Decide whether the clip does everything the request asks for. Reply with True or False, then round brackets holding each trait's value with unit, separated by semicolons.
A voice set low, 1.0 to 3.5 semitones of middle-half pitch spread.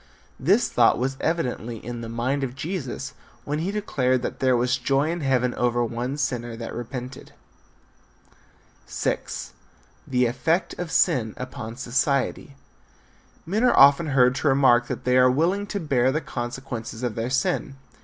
True (130 Hz; 2.7 semitones)